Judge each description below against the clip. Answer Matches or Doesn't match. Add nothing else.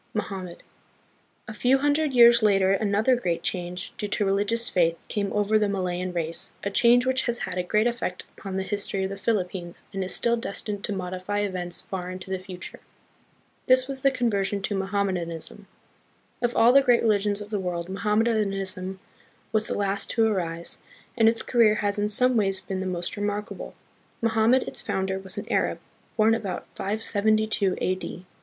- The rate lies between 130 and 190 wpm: Matches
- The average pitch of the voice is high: Matches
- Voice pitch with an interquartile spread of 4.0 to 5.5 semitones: Doesn't match